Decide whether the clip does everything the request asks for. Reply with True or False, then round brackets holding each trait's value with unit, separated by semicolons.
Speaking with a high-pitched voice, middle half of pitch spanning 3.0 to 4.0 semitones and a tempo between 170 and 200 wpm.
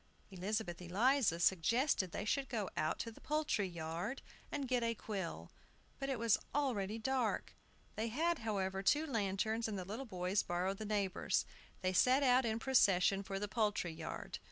False (215 Hz; 4.8 semitones; 175 wpm)